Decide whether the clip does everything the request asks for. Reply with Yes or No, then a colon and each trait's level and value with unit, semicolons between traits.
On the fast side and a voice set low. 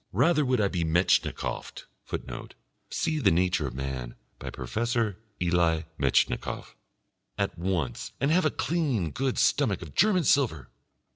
No: average, 140 wpm; very low, 95 Hz